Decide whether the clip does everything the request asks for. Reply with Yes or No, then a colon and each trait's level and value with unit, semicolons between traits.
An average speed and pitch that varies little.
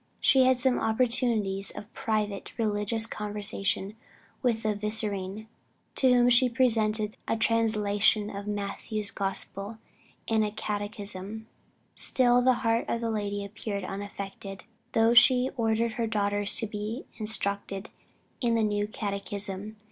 No: slow, 130 wpm; narrow, 2.1 semitones